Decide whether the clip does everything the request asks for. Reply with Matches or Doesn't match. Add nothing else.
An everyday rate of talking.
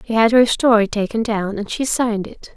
Doesn't match